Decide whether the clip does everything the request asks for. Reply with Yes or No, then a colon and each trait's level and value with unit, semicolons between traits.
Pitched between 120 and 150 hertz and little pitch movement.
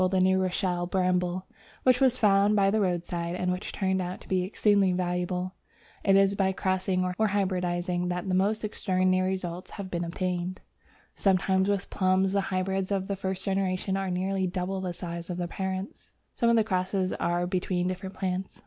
No: medium, 185 Hz; narrow, 1.2 semitones